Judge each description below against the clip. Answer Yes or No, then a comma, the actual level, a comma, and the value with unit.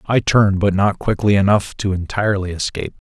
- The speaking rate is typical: Yes, average, 175 wpm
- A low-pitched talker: Yes, low, 100 Hz